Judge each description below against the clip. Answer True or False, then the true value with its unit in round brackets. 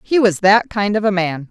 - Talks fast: True (280 wpm)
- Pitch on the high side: True (200 Hz)